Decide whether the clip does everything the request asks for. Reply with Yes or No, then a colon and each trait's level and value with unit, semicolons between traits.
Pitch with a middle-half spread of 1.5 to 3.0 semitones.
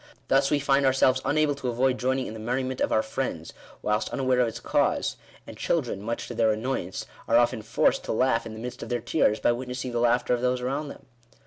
Yes: narrow, 2.4 semitones